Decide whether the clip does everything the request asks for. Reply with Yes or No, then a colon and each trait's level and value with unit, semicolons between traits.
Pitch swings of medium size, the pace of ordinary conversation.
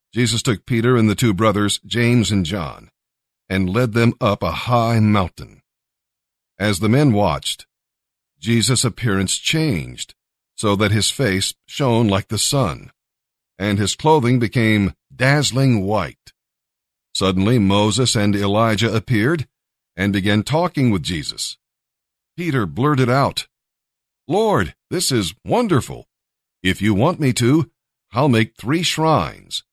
No: average, 3.9 semitones; slow, 130 wpm